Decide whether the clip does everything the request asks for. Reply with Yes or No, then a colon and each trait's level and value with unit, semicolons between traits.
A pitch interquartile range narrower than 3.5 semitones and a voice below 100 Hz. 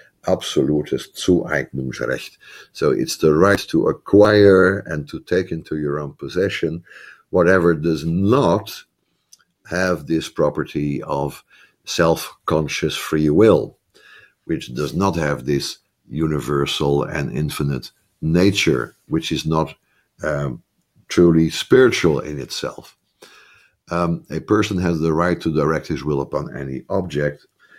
Yes: average, 2.7 semitones; very low, 80 Hz